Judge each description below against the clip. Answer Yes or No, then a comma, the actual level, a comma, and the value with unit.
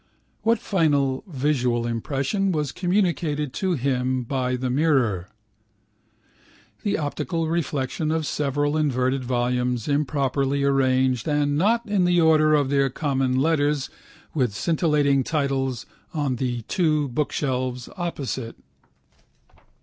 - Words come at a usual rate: No, slow, 110 wpm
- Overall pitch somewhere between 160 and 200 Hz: No, medium, 140 Hz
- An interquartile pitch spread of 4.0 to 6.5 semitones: No, average, 3.3 semitones